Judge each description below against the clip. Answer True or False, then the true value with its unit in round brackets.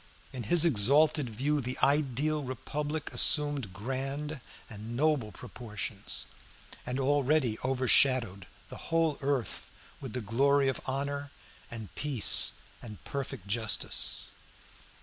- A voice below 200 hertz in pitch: True (135 Hz)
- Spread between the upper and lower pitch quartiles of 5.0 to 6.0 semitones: False (3.9 semitones)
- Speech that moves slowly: True (110 wpm)